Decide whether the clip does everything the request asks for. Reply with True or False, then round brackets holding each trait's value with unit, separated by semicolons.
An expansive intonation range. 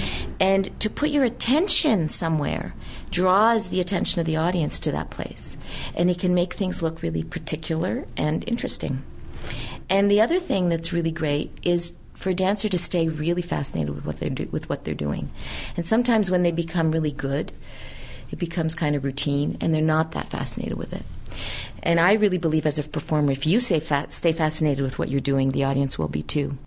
False (4.3 semitones)